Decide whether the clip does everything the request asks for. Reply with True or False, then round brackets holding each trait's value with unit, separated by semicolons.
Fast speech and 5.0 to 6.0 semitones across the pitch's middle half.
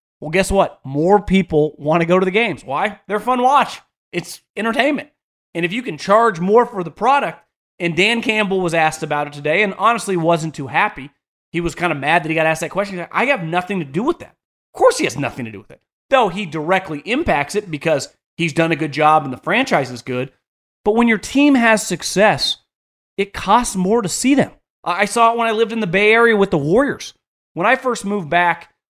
True (240 wpm; 5.5 semitones)